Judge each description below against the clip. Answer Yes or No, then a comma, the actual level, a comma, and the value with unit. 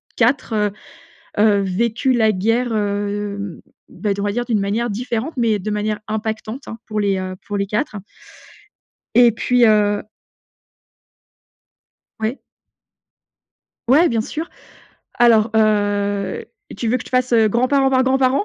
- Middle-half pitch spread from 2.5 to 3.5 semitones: Yes, average, 2.9 semitones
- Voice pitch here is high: Yes, high, 220 Hz